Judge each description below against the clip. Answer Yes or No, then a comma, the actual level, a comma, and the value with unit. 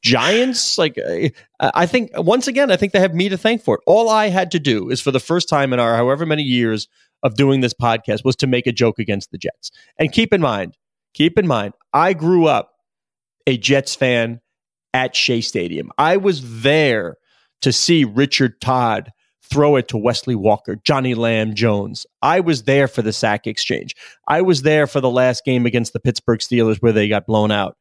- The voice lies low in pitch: Yes, low, 130 Hz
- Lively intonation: Yes, wide, 6.1 semitones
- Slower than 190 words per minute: No, fast, 205 wpm